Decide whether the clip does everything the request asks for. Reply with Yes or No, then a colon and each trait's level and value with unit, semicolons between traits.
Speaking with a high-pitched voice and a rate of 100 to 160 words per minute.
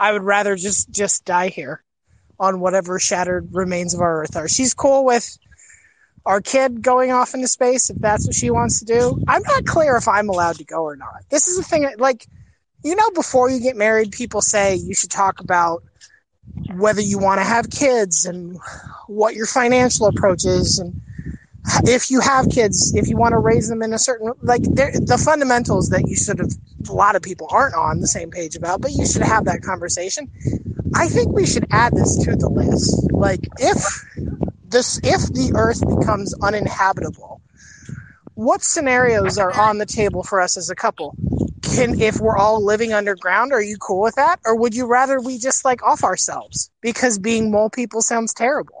No: high, 220 Hz; average, 200 wpm